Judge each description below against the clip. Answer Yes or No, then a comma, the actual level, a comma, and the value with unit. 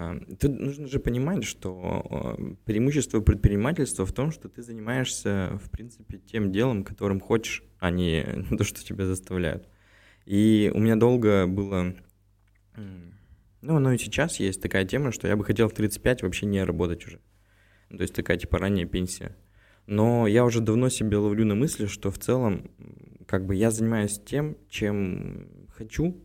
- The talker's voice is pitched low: Yes, low, 105 Hz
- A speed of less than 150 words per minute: No, fast, 160 wpm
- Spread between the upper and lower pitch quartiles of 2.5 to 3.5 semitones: Yes, average, 3.1 semitones